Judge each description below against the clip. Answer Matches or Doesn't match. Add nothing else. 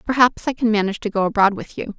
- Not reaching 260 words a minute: Doesn't match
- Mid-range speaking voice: Doesn't match